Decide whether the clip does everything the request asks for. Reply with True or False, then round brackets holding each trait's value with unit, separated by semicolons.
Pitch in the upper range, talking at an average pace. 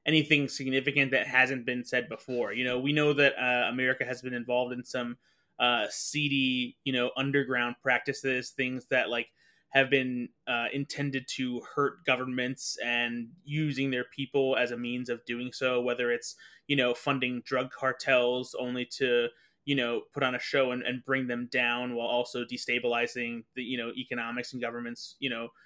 False (125 Hz; 180 wpm)